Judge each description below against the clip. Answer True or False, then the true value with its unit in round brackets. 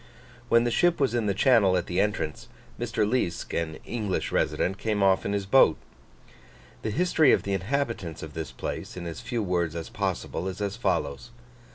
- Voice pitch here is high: False (100 Hz)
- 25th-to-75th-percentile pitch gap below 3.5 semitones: False (5.0 semitones)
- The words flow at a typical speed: True (190 wpm)